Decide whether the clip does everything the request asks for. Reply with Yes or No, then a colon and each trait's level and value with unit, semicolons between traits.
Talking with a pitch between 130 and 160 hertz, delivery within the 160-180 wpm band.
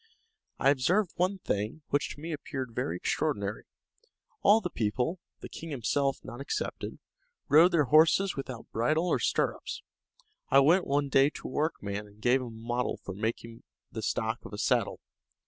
Yes: medium, 140 Hz; average, 170 wpm